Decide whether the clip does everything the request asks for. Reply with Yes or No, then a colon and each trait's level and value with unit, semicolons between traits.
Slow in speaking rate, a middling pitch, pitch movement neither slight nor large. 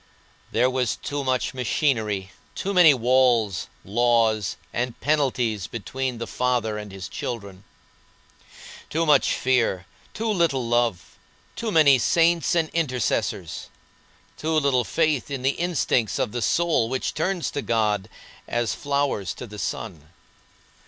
No: slow, 130 wpm; low, 125 Hz; average, 4.8 semitones